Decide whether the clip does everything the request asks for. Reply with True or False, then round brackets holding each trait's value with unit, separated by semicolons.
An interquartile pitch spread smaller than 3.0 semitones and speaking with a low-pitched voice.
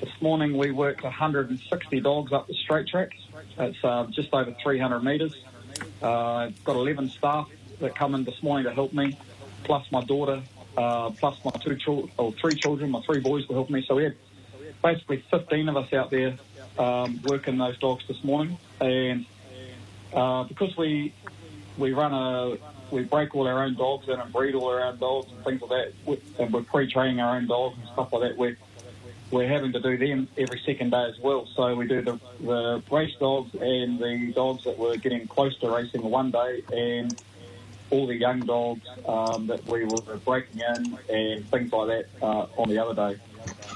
True (2.6 semitones; 125 Hz)